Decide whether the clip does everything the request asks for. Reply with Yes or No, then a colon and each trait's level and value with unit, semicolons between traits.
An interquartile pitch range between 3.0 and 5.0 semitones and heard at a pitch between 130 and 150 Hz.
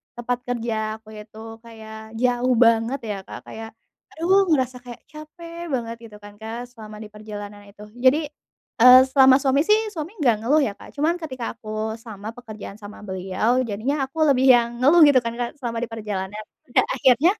No: average, 3.5 semitones; high, 235 Hz